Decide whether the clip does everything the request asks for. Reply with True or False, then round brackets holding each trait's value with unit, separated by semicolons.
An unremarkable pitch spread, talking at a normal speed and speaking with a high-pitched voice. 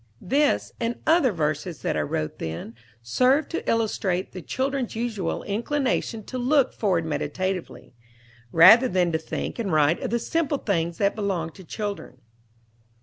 False (6.8 semitones; 150 wpm; 200 Hz)